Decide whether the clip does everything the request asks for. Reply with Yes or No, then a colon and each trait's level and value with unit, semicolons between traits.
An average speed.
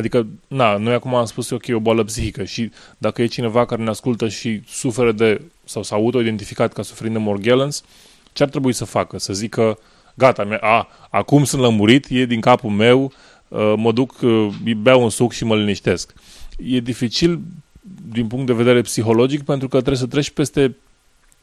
Yes: average, 195 wpm